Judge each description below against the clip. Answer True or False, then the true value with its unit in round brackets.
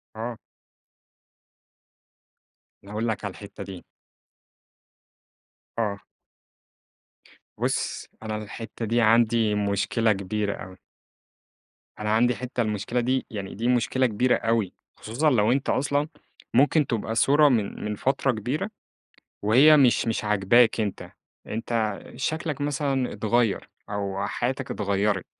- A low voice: True (115 Hz)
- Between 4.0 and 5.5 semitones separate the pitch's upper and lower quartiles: False (3.4 semitones)